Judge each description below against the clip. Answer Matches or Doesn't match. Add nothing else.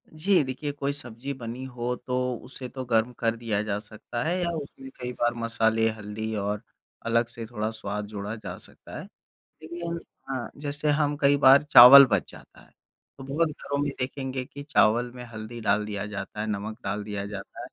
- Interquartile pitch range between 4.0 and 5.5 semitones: Matches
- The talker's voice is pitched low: Matches